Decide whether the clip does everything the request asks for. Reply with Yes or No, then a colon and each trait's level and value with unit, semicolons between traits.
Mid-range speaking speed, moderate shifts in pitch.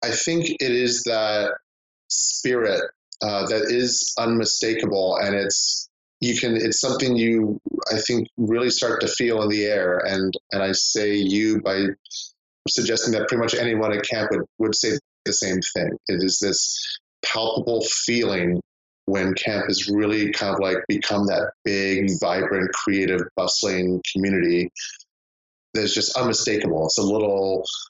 Yes: average, 150 wpm; average, 3.2 semitones